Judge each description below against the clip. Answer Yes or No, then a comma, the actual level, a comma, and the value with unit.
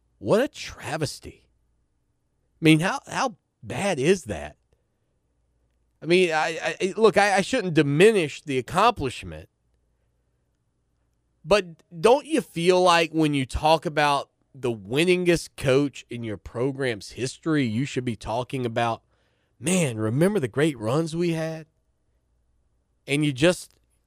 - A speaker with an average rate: No, slow, 130 wpm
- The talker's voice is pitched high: No, low, 135 Hz